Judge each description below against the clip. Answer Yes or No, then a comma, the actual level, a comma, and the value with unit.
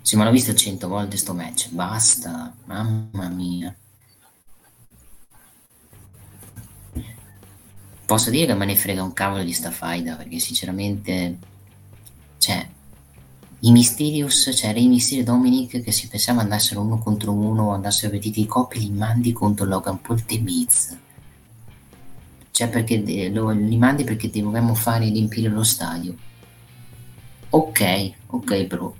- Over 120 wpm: Yes, average, 130 wpm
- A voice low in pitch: Yes, low, 105 Hz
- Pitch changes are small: No, average, 3.6 semitones